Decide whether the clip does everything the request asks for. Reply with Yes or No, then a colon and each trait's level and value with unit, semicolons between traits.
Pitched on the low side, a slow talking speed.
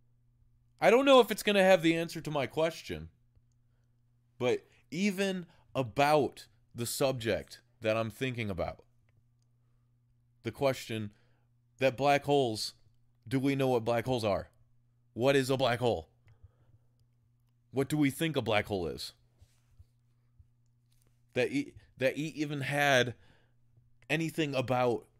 Yes: low, 120 Hz; slow, 130 wpm